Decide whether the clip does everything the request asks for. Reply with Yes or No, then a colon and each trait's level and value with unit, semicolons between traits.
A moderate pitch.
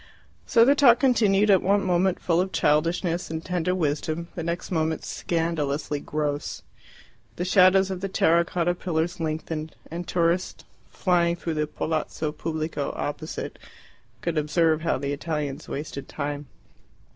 Yes: medium, 165 Hz